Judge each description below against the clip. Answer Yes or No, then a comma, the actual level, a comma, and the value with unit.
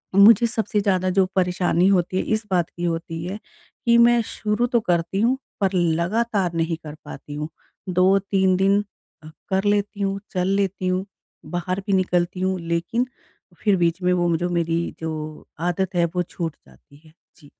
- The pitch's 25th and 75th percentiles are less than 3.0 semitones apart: Yes, narrow, 2.5 semitones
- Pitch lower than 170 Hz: No, medium, 185 Hz